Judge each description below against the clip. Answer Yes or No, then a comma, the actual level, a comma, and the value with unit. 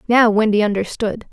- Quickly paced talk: No, slow, 135 wpm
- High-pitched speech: Yes, high, 215 Hz